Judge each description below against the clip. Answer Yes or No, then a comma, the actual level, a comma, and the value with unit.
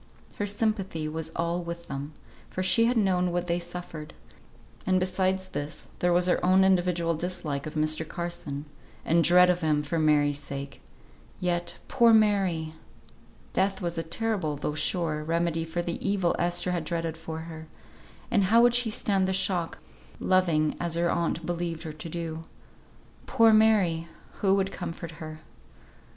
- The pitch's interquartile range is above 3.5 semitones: No, average, 2.7 semitones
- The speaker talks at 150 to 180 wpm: Yes, average, 165 wpm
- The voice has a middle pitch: Yes, medium, 170 Hz